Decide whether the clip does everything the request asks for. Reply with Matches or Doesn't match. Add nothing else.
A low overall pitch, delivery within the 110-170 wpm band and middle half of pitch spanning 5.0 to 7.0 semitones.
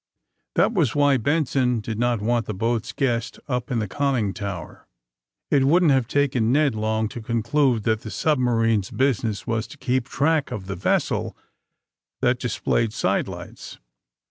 Doesn't match